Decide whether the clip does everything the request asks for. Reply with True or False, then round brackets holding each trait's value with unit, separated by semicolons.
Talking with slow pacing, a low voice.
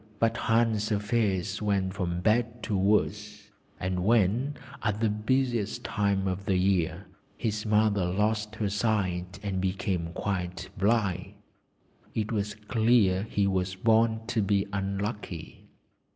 True (130 wpm; 105 Hz)